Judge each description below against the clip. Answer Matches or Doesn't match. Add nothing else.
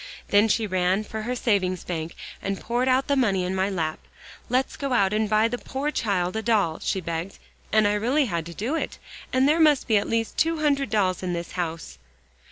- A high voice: Matches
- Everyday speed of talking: Doesn't match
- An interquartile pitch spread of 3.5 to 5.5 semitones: Matches